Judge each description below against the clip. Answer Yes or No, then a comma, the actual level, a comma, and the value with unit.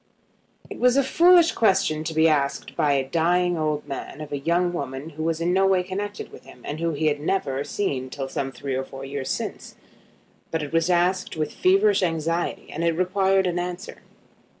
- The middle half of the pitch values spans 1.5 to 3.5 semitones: No, average, 4.3 semitones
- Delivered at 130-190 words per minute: No, fast, 205 wpm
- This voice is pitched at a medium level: Yes, medium, 165 Hz